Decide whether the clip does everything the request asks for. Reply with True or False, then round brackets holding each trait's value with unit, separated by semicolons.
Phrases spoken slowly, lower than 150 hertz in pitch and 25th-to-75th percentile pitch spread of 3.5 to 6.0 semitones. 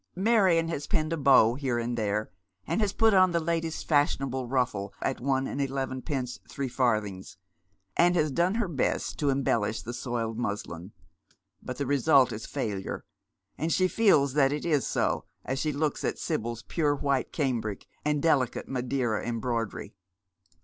False (165 wpm; 135 Hz; 4.8 semitones)